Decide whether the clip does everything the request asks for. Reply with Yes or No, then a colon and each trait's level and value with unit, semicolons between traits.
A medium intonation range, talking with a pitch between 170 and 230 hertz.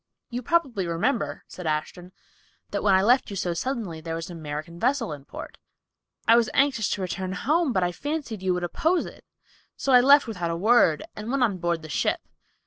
No: wide, 6.7 semitones; high, 190 Hz